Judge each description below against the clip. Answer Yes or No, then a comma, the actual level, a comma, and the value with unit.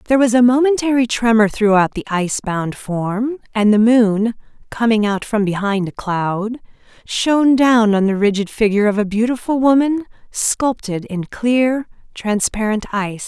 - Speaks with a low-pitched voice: No, high, 225 Hz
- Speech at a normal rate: Yes, average, 155 wpm